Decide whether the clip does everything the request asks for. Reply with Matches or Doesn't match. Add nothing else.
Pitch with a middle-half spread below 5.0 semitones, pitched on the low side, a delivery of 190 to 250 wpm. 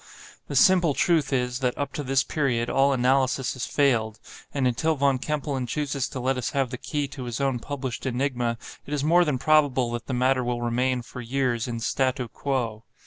Matches